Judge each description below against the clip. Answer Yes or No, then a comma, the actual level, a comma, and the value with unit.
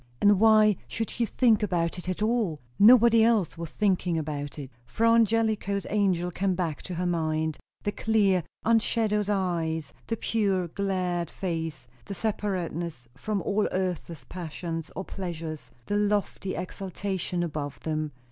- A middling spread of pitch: Yes, average, 4.1 semitones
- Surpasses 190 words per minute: No, average, 145 wpm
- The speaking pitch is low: No, medium, 185 Hz